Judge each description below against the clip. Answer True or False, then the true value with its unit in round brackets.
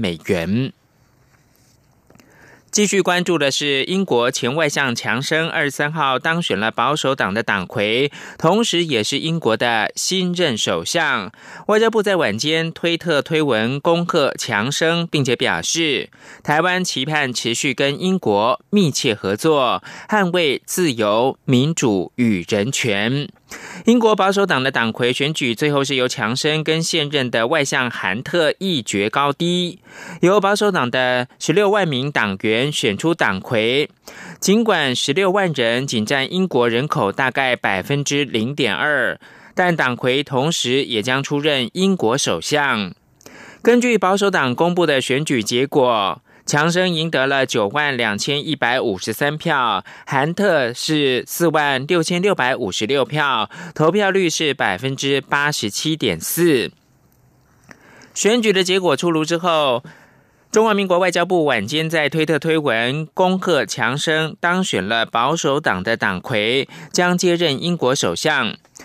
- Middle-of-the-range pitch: True (155 Hz)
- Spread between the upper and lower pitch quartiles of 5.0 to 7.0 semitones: True (5.6 semitones)